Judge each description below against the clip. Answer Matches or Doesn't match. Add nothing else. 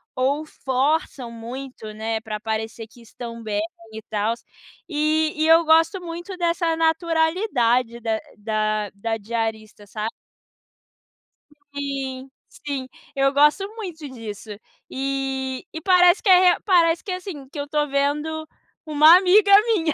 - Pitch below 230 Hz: Doesn't match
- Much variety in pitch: Matches